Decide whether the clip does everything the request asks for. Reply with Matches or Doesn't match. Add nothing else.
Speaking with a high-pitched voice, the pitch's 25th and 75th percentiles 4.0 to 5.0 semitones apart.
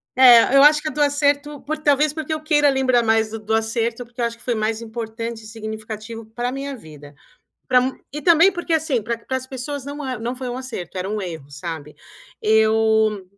Matches